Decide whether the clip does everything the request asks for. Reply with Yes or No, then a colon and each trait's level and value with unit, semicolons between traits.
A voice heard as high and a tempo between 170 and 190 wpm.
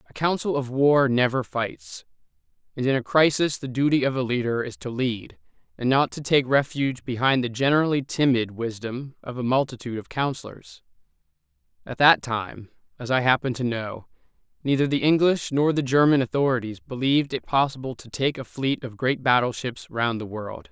No: low, 130 Hz; average, 175 wpm